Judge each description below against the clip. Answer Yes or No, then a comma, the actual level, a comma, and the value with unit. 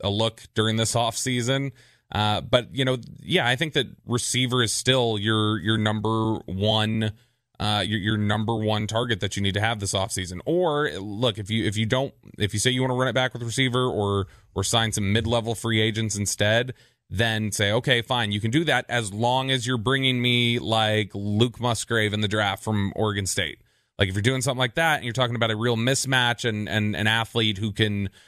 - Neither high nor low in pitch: No, low, 115 Hz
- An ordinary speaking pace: No, fast, 225 wpm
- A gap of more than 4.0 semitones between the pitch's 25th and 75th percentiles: No, average, 2.9 semitones